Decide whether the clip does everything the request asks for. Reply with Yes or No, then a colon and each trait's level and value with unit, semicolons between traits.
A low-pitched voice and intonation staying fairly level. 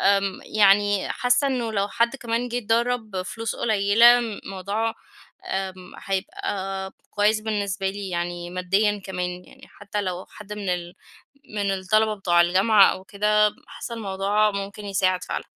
No: high, 200 Hz; narrow, 2.3 semitones